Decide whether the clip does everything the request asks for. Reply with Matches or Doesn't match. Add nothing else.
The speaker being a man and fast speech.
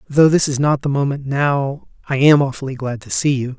Matches